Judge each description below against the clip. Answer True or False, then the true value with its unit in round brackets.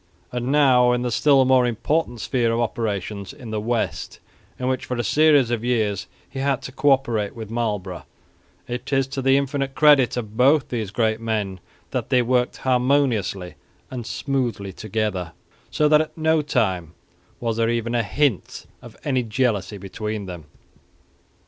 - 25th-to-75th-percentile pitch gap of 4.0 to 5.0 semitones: False (3.6 semitones)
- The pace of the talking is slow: False (170 wpm)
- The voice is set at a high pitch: False (120 Hz)